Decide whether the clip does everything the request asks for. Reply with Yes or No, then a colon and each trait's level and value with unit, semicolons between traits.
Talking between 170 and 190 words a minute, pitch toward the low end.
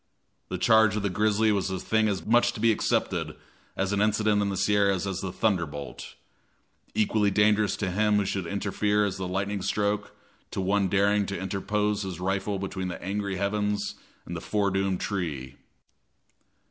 Yes: average, 175 wpm; low, 100 Hz